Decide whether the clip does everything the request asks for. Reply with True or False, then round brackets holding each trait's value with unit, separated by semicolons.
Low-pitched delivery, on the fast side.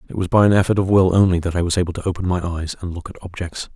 True (90 Hz; 320 wpm)